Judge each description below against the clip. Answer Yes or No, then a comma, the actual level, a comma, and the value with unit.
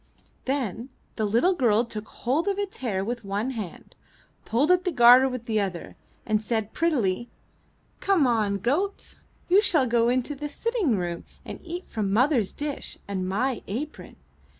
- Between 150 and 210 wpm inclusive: Yes, average, 165 wpm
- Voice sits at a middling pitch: No, high, 240 Hz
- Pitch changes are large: Yes, wide, 5.7 semitones